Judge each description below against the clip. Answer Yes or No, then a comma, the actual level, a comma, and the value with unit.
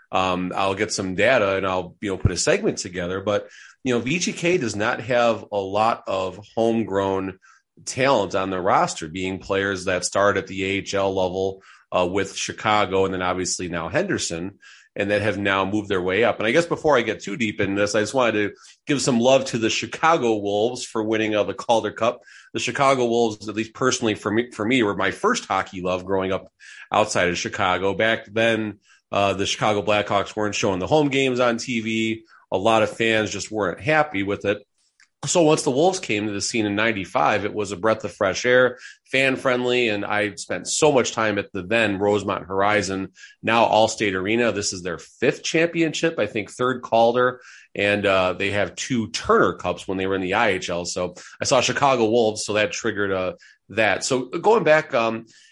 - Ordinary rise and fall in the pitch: Yes, average, 3.5 semitones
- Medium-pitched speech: No, low, 105 Hz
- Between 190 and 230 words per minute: Yes, fast, 205 wpm